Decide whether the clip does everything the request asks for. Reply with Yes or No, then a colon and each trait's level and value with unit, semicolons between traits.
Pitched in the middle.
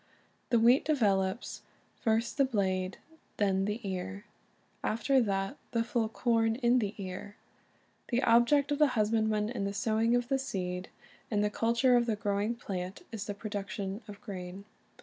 No: high, 215 Hz